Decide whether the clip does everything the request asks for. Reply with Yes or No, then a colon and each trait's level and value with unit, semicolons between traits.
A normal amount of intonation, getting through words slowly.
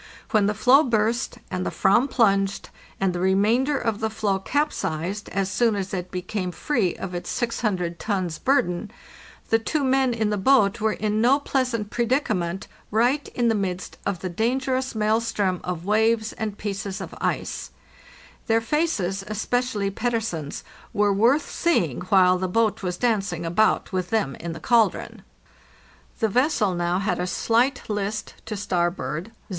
No: average, 4.0 semitones; average, 165 wpm